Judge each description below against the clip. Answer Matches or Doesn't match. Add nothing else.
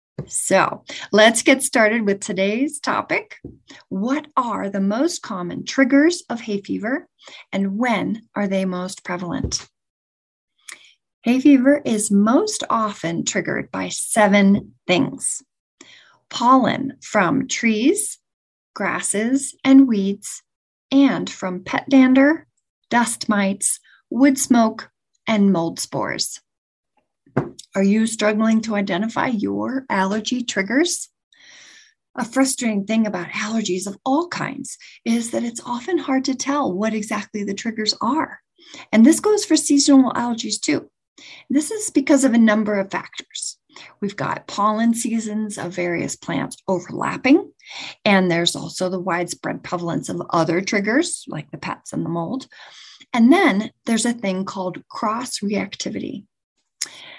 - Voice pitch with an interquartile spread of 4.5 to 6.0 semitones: Matches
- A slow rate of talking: Matches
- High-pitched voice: Matches